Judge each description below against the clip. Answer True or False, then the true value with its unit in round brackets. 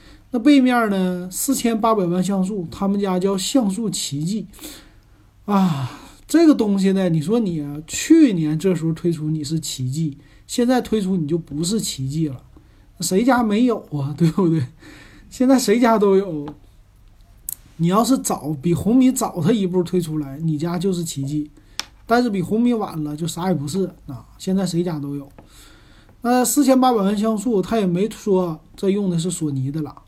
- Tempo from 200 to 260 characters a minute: True (245 characters per minute)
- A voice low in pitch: False (180 Hz)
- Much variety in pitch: True (6.1 semitones)